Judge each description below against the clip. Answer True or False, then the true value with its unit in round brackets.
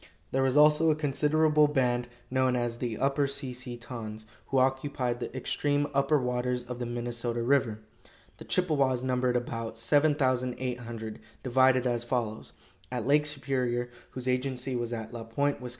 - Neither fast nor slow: True (155 wpm)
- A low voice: True (125 Hz)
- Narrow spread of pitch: True (2.3 semitones)